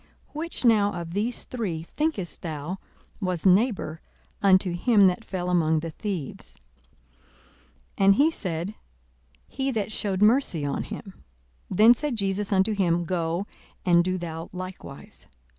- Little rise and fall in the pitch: No, average, 3.8 semitones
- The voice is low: No, high, 190 Hz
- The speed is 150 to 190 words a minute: No, average, 140 wpm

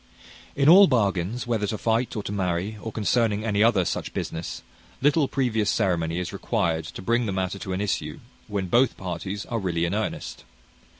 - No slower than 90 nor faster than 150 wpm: No, average, 185 wpm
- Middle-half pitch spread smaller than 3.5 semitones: No, average, 4.1 semitones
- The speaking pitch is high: No, low, 105 Hz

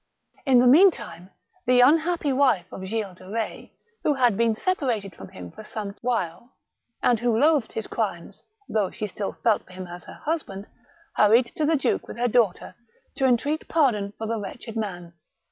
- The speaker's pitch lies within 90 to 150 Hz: No, high, 225 Hz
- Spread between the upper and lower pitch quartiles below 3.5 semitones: No, average, 4.7 semitones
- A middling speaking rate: Yes, average, 180 wpm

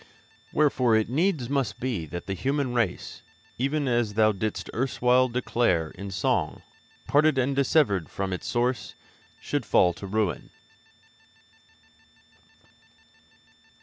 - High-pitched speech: No, low, 120 Hz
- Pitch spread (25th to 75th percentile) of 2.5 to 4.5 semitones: No, average, 5.3 semitones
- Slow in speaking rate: Yes, slow, 115 wpm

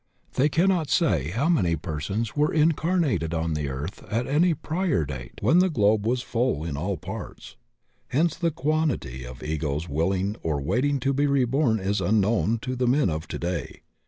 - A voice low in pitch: Yes, low, 110 Hz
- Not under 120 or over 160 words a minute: No, average, 175 wpm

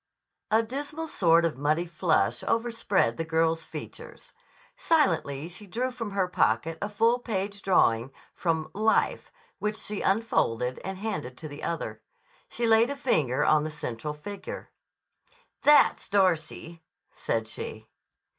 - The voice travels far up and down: Yes, wide, 6.3 semitones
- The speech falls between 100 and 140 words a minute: Yes, slow, 135 wpm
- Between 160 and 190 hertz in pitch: Yes, medium, 185 Hz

